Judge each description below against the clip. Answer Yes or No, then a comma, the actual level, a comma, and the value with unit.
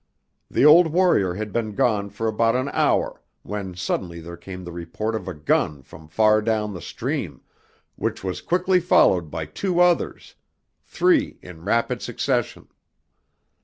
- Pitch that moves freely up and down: Yes, wide, 6.7 semitones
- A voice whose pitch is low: Yes, low, 105 Hz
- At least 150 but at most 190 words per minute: Yes, average, 155 wpm